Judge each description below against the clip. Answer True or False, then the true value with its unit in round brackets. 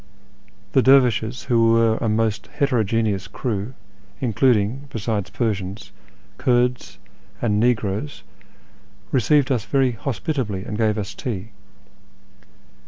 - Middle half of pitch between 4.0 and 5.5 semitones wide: False (3.3 semitones)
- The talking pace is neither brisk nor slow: False (100 wpm)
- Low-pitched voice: True (115 Hz)